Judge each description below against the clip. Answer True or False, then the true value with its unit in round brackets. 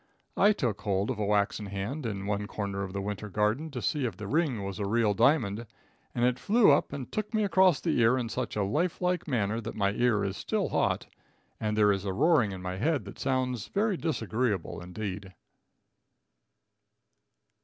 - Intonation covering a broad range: True (5.8 semitones)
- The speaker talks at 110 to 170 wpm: False (195 wpm)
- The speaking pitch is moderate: False (110 Hz)